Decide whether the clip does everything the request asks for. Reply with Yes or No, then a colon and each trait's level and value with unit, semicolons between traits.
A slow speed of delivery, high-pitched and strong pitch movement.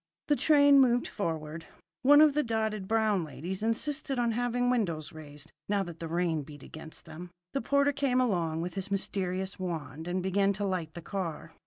No: average, 185 wpm; high, 195 Hz; wide, 6.7 semitones